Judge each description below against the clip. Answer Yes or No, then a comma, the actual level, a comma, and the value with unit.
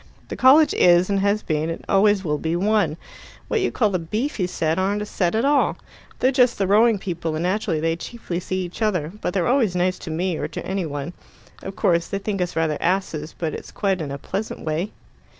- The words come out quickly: Yes, fast, 225 wpm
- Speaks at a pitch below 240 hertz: Yes, medium, 185 Hz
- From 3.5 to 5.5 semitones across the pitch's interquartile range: Yes, average, 4.1 semitones